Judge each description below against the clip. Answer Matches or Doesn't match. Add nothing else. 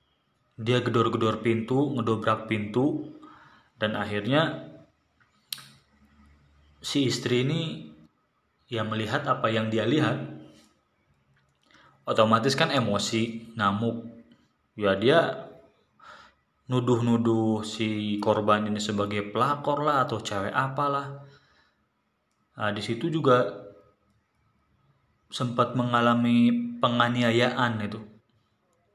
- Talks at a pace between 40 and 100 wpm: Matches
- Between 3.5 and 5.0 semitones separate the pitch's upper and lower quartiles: Doesn't match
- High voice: Doesn't match